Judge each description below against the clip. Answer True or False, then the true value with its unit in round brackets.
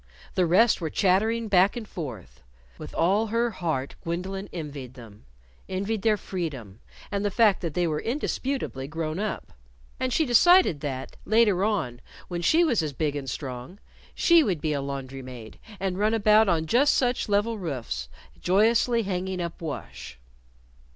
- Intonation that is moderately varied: False (7.0 semitones)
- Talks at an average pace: True (165 wpm)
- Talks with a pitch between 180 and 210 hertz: True (185 Hz)